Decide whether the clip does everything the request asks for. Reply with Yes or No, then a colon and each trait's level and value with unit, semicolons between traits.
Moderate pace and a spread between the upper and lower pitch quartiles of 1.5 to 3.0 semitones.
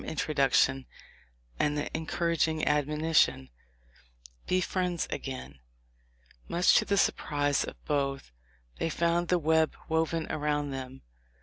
No: slow, 115 wpm; average, 2.7 semitones